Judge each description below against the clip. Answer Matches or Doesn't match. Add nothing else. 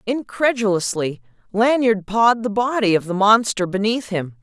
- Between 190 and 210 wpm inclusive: Doesn't match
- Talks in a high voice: Matches